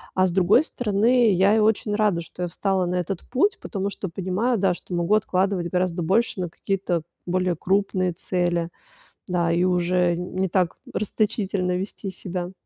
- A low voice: No, medium, 185 Hz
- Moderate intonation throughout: No, narrow, 2.2 semitones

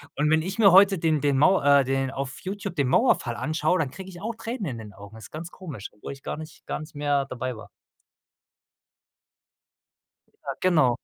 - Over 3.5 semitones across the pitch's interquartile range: Yes, wide, 5.6 semitones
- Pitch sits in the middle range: Yes, medium, 150 Hz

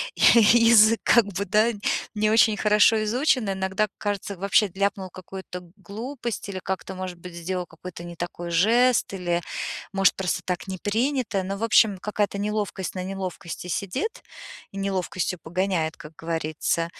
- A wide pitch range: No, average, 2.8 semitones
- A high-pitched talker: Yes, high, 195 Hz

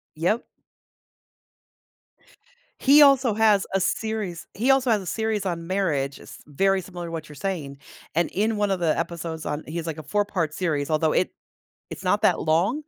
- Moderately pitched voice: Yes, medium, 180 Hz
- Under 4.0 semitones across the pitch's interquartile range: No, average, 4.8 semitones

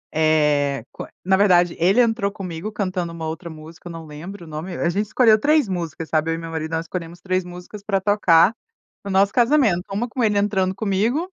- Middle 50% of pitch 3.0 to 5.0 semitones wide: Yes, average, 3.9 semitones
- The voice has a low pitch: No, medium, 185 Hz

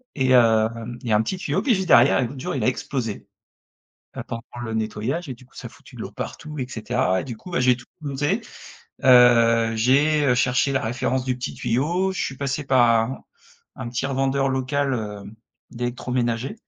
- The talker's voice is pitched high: No, low, 125 Hz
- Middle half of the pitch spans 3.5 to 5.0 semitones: No, average, 2.9 semitones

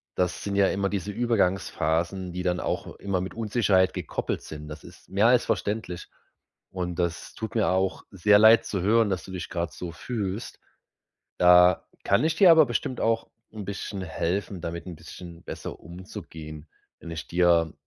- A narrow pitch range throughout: No, average, 3.1 semitones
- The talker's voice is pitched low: Yes, very low, 95 Hz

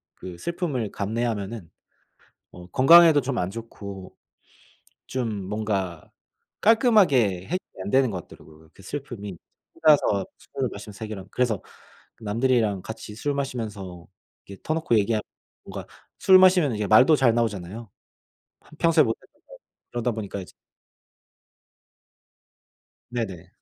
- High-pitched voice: No, low, 110 Hz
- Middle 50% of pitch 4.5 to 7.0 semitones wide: Yes, average, 5.3 semitones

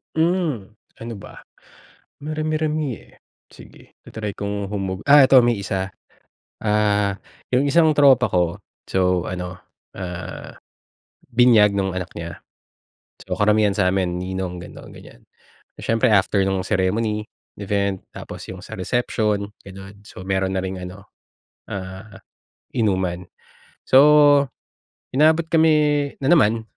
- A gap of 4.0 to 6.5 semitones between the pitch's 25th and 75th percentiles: Yes, average, 5.1 semitones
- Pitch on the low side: Yes, low, 105 Hz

